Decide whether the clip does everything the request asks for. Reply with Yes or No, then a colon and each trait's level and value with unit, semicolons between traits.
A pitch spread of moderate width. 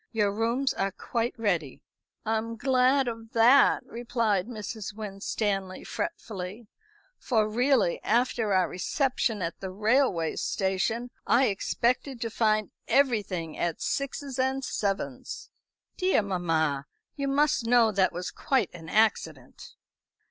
Yes: average, 4.4 semitones